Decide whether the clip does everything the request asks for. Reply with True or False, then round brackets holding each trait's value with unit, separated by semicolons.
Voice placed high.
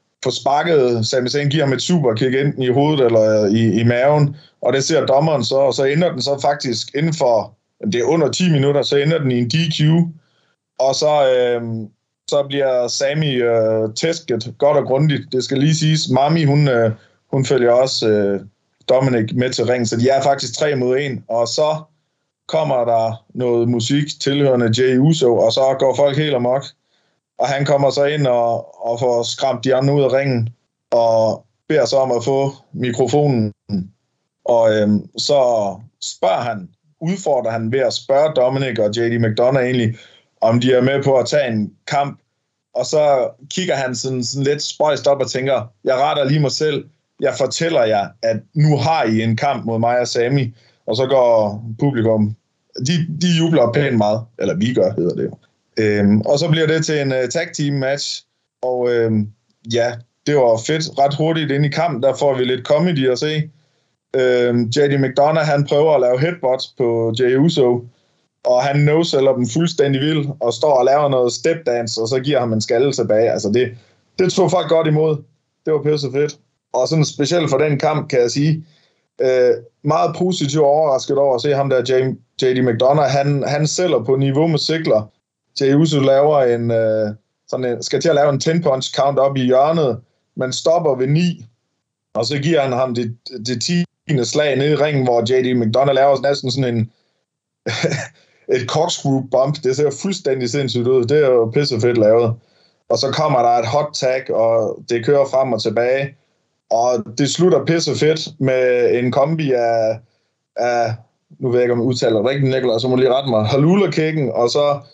False (135 Hz)